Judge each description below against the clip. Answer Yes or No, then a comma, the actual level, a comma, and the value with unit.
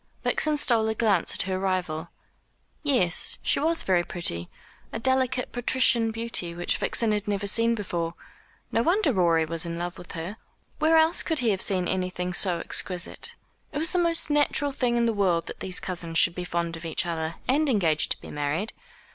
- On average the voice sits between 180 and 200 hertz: Yes, high, 190 Hz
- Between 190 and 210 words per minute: Yes, average, 195 wpm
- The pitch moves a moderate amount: No, wide, 6.0 semitones